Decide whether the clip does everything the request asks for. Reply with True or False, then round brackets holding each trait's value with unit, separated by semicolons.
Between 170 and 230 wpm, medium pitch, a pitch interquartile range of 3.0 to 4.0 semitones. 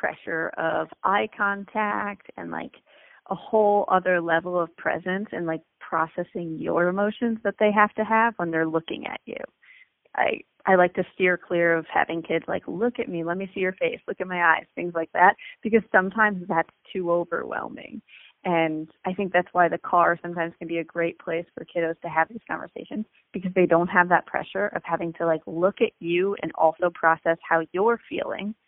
True (200 wpm; 180 Hz; 3.6 semitones)